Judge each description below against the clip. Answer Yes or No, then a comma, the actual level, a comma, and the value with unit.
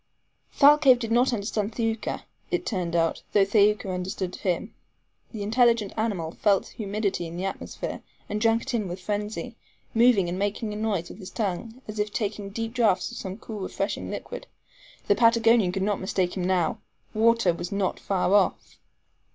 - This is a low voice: No, high, 205 Hz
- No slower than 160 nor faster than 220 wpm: Yes, average, 175 wpm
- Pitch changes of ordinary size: Yes, average, 3.2 semitones